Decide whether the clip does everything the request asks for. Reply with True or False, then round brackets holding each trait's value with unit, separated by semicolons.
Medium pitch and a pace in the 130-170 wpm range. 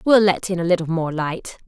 False (175 Hz; 250 wpm)